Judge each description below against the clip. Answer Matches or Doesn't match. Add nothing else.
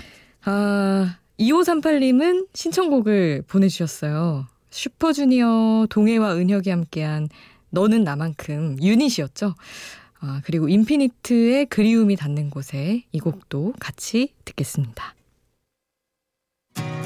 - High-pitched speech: Matches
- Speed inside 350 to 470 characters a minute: Doesn't match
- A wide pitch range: Matches